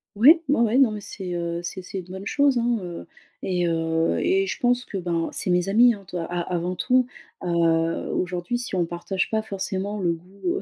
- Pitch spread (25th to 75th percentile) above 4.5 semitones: Yes, average, 5.1 semitones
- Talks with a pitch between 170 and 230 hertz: Yes, high, 190 Hz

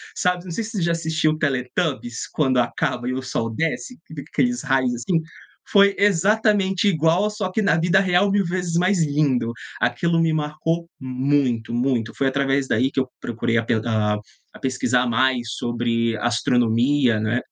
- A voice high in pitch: No, medium, 145 Hz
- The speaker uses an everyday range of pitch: No, wide, 6.2 semitones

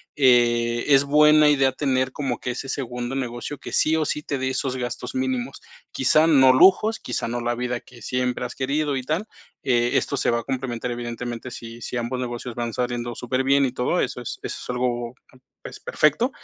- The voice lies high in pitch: No, low, 125 Hz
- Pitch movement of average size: No, narrow, 2.1 semitones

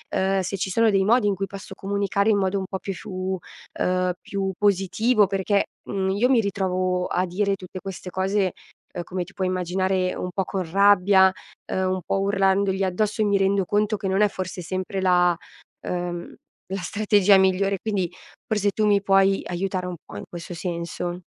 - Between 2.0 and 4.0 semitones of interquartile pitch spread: No, narrow, 1.6 semitones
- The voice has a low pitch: No, high, 190 Hz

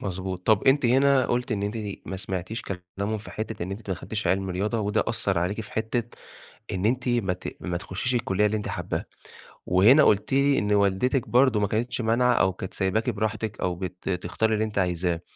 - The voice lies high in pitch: No, low, 105 Hz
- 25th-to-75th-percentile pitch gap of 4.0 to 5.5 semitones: No, average, 3.6 semitones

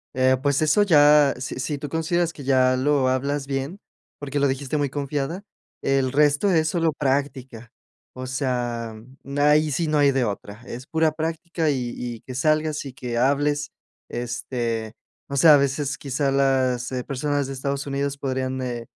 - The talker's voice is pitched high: No, medium, 140 Hz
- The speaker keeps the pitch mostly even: Yes, narrow, 2.3 semitones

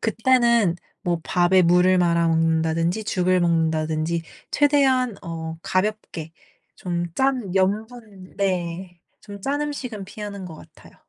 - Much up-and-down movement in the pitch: No, average, 4.4 semitones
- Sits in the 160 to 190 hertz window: Yes, medium, 185 Hz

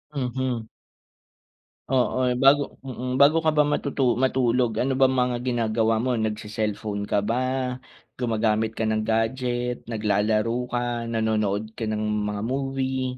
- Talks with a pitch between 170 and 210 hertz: No, low, 115 Hz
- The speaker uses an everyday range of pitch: Yes, average, 3.0 semitones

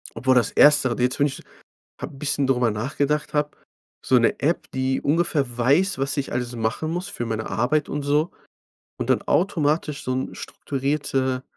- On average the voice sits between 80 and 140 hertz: Yes, low, 135 Hz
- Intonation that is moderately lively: Yes, average, 3.0 semitones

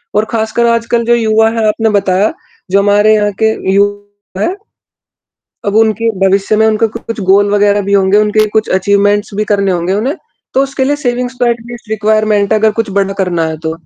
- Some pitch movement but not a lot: No, narrow, 2.0 semitones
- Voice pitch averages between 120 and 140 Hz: No, high, 210 Hz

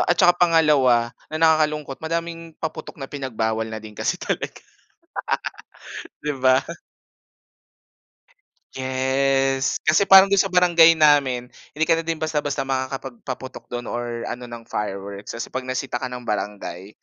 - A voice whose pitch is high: No, low, 135 Hz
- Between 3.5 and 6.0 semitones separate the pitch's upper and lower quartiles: Yes, average, 4.8 semitones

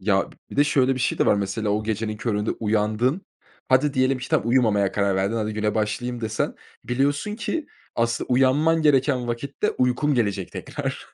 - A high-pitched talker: No, low, 120 Hz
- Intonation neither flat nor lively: Yes, average, 3.9 semitones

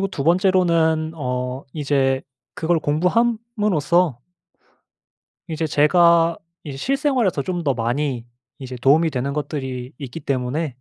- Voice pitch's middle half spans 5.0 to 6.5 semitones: No, average, 4.6 semitones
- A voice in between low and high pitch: Yes, medium, 155 Hz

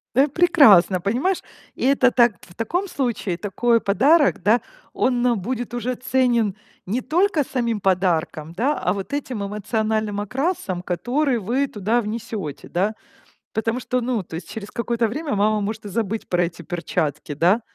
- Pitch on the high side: Yes, high, 225 Hz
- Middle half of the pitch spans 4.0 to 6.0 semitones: Yes, average, 4.4 semitones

